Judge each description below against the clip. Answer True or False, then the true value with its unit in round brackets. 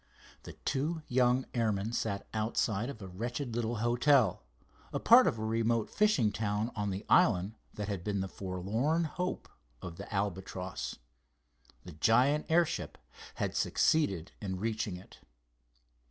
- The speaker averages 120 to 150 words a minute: True (140 wpm)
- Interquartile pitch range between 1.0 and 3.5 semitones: False (4.1 semitones)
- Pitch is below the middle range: True (110 Hz)